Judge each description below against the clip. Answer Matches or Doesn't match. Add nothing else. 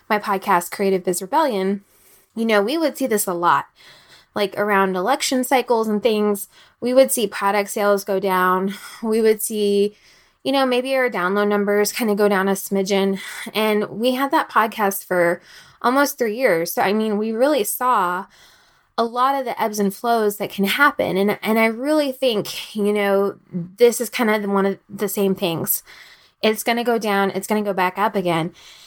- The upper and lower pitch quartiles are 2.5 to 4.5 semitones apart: Matches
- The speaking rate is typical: Matches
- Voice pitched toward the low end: Doesn't match